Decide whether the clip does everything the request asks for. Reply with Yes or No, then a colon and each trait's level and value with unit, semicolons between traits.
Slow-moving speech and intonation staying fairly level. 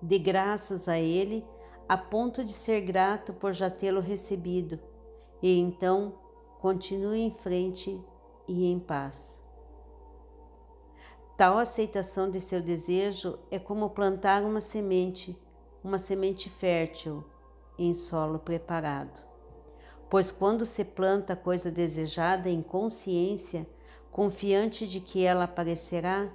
Yes: slow, 115 wpm; narrow, 2.2 semitones